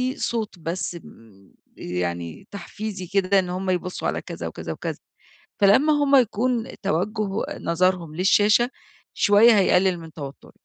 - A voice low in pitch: No, high, 190 Hz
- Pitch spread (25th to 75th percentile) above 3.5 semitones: Yes, average, 4.1 semitones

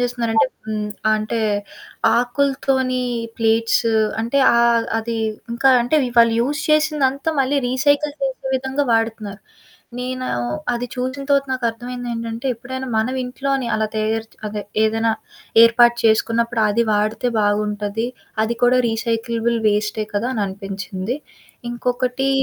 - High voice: Yes, high, 235 Hz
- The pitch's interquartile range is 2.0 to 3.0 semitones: Yes, average, 2.7 semitones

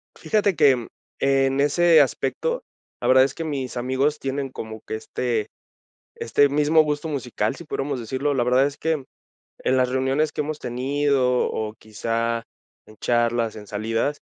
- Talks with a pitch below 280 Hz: Yes, low, 135 Hz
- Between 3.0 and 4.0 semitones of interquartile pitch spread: Yes, average, 3.5 semitones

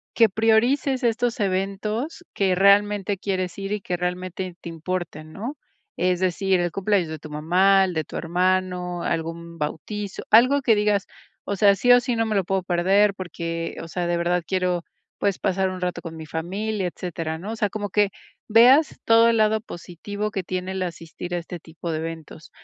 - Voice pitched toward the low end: No, medium, 185 Hz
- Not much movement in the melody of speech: No, average, 3.2 semitones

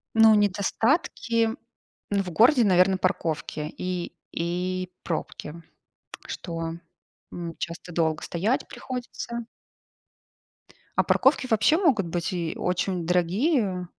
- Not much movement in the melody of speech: No, average, 4.6 semitones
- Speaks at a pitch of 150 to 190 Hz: Yes, medium, 185 Hz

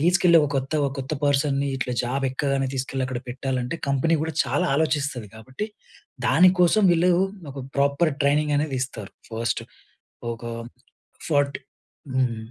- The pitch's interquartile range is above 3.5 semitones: No, average, 2.9 semitones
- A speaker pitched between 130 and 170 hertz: Yes, medium, 140 Hz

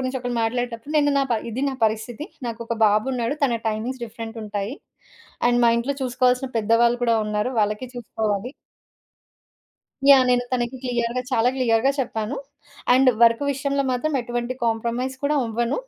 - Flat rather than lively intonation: Yes, narrow, 2.3 semitones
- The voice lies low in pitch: No, high, 240 Hz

